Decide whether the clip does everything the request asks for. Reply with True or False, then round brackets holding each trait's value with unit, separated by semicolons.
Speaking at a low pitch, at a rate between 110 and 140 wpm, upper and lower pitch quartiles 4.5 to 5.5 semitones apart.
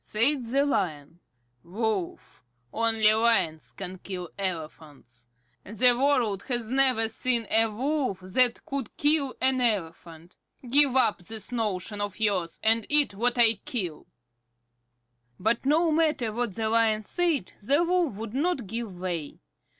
False (225 Hz; 135 wpm; 5.2 semitones)